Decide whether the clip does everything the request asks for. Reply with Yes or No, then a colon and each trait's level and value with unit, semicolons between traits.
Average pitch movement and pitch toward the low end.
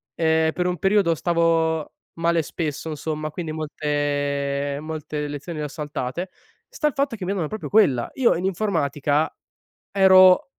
No: average, 3.7 semitones; medium, 160 Hz